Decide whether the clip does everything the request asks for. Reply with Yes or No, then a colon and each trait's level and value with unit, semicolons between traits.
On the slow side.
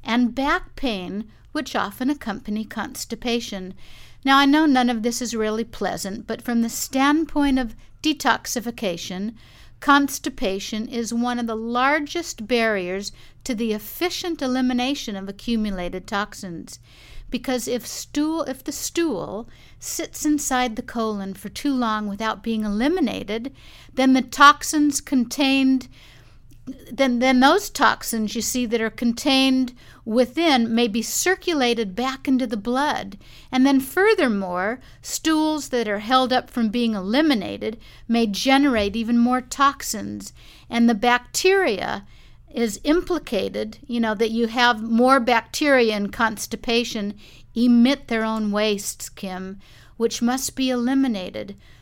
Yes: slow, 130 wpm